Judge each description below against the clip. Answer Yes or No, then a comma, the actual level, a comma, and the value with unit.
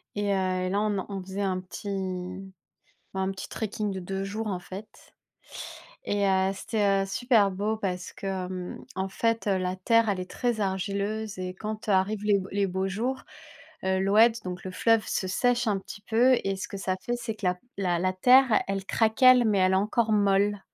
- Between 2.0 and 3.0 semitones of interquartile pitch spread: Yes, narrow, 2.4 semitones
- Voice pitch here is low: No, high, 195 Hz